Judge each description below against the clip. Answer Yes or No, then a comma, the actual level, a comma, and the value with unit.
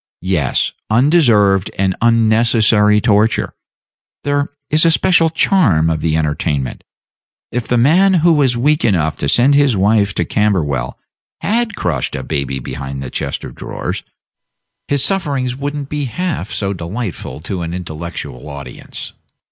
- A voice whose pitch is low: Yes, low, 105 Hz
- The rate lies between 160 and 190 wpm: No, average, 145 wpm